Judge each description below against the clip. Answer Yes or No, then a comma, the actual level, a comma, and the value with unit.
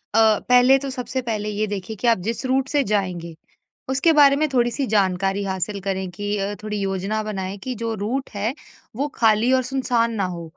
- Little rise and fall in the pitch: No, average, 4.4 semitones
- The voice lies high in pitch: Yes, high, 215 Hz